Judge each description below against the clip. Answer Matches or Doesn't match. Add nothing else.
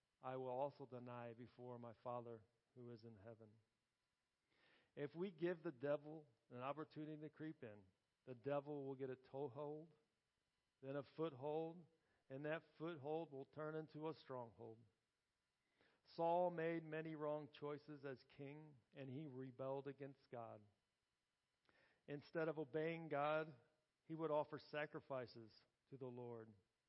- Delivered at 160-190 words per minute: Doesn't match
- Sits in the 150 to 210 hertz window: Doesn't match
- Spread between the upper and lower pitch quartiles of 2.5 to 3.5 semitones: Doesn't match